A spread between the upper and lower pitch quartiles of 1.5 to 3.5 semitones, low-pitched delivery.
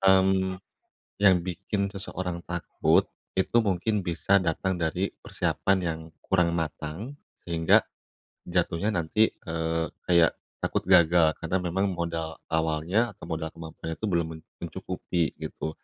Yes: average, 2.7 semitones; very low, 85 Hz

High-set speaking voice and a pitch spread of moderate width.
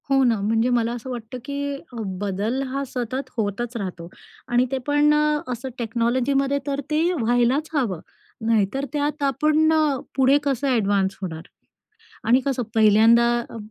Yes: very high, 250 Hz; average, 3.8 semitones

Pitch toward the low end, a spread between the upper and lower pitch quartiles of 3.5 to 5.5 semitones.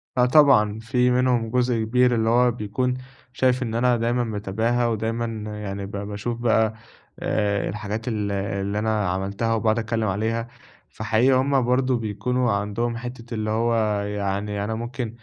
No: low, 115 Hz; average, 2.8 semitones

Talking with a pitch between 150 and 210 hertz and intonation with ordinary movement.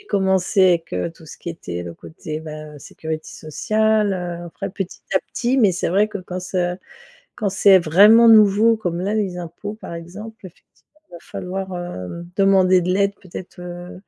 Yes: medium, 185 Hz; average, 3.0 semitones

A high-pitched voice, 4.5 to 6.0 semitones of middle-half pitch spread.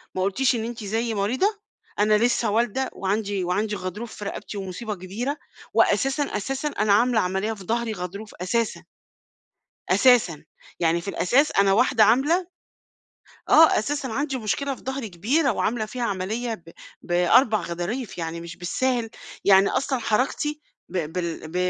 Yes: high, 215 Hz; average, 4.8 semitones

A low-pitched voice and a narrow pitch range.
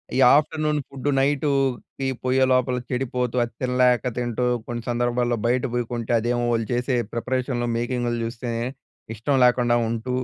Yes: low, 125 Hz; narrow, 1.4 semitones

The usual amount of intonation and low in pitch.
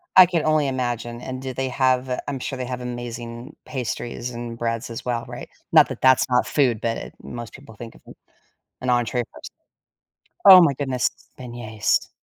No: narrow, 1.8 semitones; low, 125 Hz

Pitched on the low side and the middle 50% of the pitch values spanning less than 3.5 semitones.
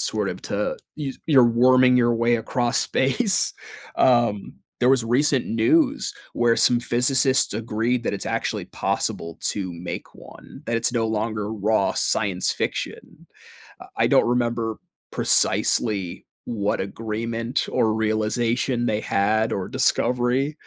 Yes: low, 115 Hz; narrow, 2.4 semitones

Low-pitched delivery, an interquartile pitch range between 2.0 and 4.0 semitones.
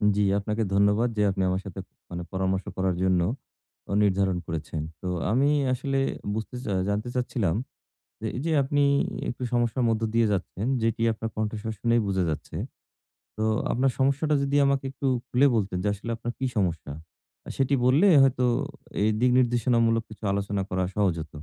No: low, 110 Hz; average, 4.5 semitones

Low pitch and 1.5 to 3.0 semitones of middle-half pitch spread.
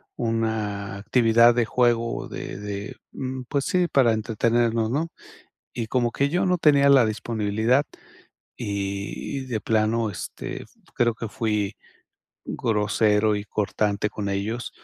Yes: low, 115 Hz; narrow, 2.6 semitones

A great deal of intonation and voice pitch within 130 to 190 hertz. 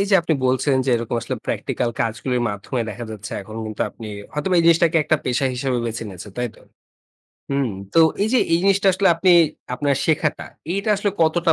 Yes: wide, 6.2 semitones; low, 135 Hz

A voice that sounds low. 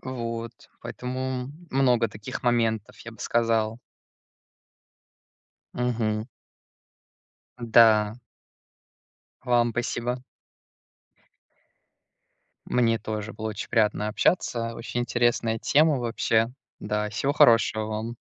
Yes: low, 115 Hz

